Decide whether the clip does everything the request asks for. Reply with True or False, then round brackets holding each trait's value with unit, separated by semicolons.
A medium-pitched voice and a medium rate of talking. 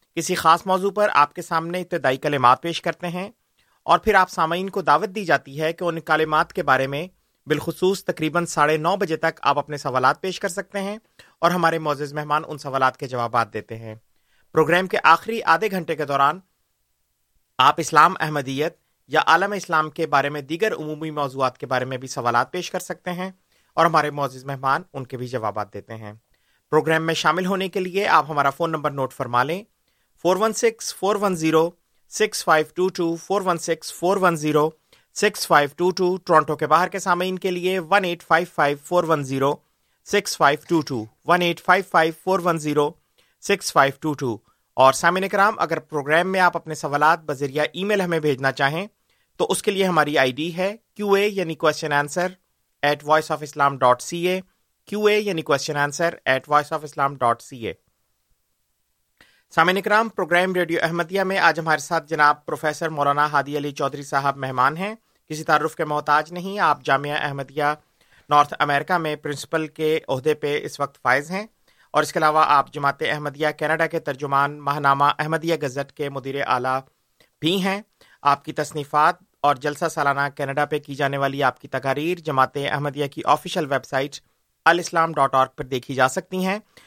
False (155 Hz; 195 wpm)